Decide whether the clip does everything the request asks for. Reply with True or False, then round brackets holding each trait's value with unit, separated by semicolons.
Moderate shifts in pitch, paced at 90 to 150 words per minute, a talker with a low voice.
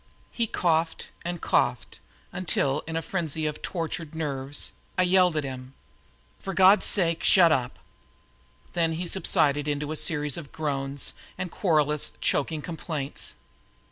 False (3.1 semitones; 140 wpm; 160 Hz)